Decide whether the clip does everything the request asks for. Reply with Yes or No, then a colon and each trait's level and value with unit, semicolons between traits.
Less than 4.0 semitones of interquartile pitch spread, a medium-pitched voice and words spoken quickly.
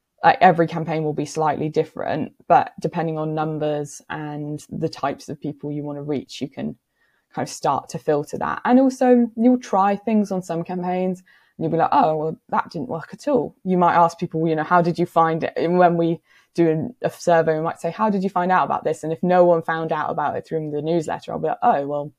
Yes: average, 2.8 semitones; medium, 165 Hz; fast, 245 wpm